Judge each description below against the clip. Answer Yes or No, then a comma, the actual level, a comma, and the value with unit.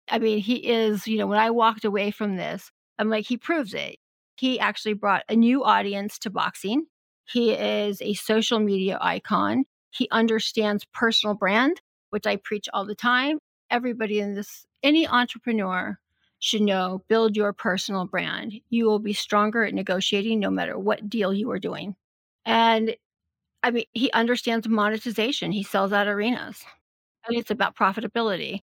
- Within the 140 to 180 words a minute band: Yes, average, 165 wpm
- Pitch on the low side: No, high, 220 Hz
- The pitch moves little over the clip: Yes, narrow, 2.3 semitones